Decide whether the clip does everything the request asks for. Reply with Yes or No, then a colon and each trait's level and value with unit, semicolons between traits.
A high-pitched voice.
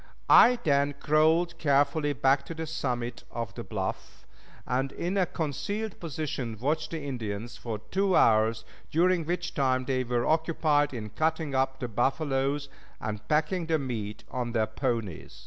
No: medium, 140 Hz